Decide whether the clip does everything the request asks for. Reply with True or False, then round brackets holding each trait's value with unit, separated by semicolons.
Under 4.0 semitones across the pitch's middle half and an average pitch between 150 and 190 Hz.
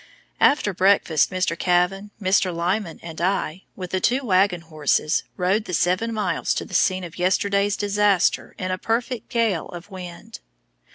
True (2.5 semitones; 185 Hz)